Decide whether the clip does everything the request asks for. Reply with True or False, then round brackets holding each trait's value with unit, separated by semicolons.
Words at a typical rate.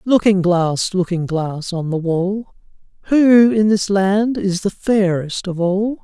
True (160 wpm)